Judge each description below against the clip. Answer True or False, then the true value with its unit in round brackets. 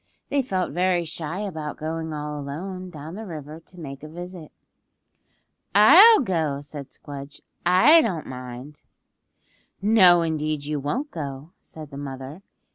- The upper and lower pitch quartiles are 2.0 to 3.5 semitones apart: False (4.1 semitones)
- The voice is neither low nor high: True (160 Hz)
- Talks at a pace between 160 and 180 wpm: False (140 wpm)